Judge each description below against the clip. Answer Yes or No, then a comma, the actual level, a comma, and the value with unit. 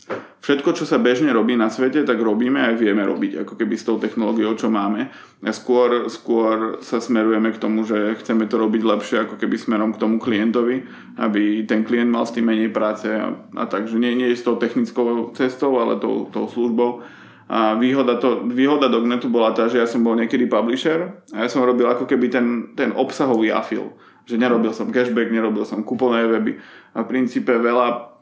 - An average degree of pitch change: No, narrow, 1.8 semitones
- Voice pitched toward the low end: Yes, low, 120 Hz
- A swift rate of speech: Yes, fast, 200 wpm